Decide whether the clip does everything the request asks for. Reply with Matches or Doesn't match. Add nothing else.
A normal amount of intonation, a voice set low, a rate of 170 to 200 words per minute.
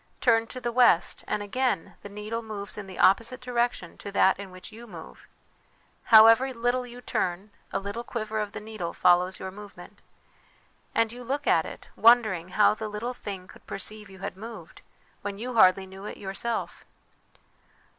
Doesn't match